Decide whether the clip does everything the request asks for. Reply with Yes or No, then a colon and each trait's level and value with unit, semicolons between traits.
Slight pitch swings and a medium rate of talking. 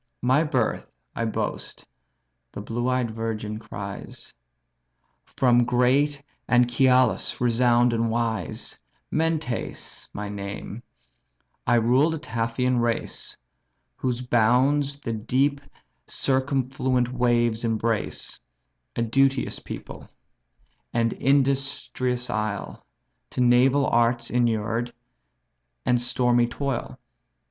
No: narrow, 2.2 semitones; slow, 95 wpm